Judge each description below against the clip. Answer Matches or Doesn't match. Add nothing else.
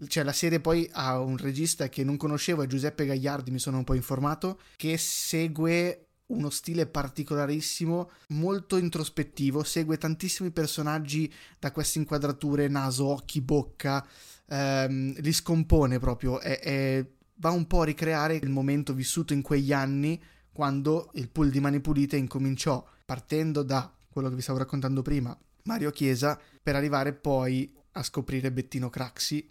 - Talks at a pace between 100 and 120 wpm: Doesn't match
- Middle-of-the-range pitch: Matches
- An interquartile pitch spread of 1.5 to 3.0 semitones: Matches